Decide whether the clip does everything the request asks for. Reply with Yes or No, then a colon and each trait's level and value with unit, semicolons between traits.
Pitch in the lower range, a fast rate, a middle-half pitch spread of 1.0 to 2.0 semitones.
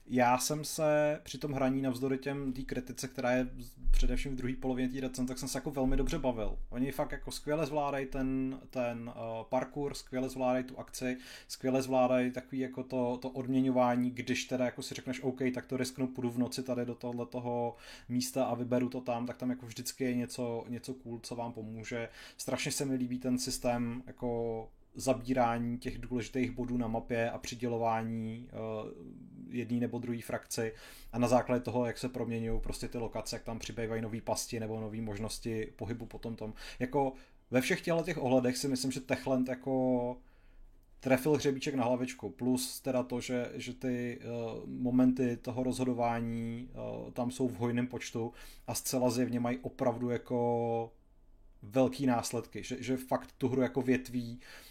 Yes: low, 125 Hz; fast, 180 wpm; narrow, 1.6 semitones